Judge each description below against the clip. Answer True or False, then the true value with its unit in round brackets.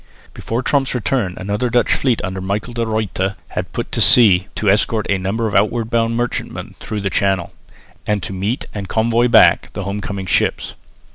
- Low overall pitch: True (105 Hz)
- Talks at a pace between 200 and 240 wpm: False (190 wpm)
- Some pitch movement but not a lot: True (3.1 semitones)